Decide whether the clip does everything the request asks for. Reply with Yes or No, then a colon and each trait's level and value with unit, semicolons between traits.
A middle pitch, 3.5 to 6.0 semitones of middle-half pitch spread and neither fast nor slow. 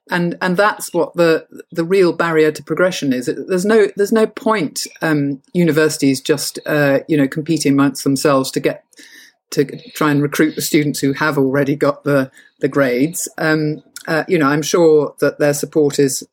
No: medium, 155 Hz; average, 3.1 semitones; average, 185 wpm